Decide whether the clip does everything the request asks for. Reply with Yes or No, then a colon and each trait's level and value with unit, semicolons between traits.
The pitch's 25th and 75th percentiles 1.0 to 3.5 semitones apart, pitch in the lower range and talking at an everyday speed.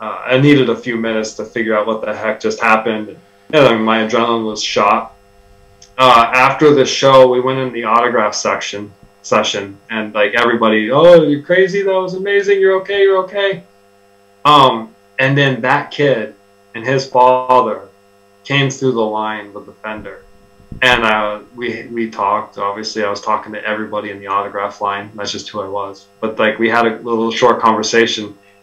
No: average, 4.0 semitones; low, 110 Hz; average, 180 wpm